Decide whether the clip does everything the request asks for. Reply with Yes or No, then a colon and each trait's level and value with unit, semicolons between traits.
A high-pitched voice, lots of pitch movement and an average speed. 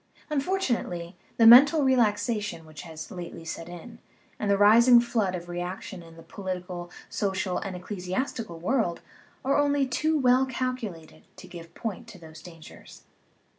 Yes: high, 200 Hz; wide, 6.0 semitones; average, 150 wpm